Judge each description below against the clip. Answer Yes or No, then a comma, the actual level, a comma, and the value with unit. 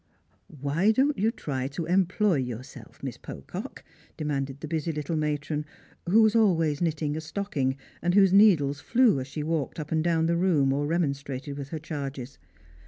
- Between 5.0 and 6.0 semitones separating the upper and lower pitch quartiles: No, average, 3.9 semitones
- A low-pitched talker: No, medium, 155 Hz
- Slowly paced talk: No, average, 180 wpm